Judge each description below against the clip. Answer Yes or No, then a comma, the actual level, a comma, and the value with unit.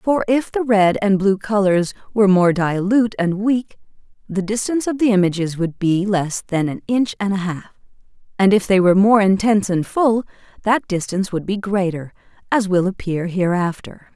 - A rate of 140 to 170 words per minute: No, average, 180 wpm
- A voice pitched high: Yes, high, 200 Hz